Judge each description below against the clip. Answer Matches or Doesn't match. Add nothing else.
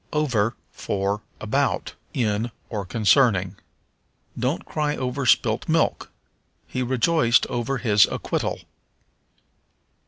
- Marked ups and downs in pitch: Doesn't match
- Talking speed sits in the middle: Doesn't match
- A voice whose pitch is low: Matches